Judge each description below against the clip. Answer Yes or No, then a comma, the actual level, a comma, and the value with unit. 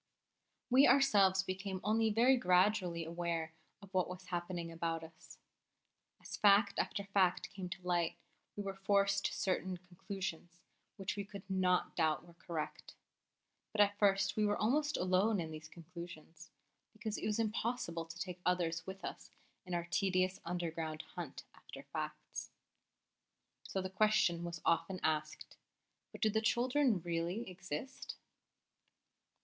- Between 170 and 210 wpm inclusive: No, average, 145 wpm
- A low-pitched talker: No, medium, 185 Hz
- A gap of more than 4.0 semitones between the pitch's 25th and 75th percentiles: No, average, 3.1 semitones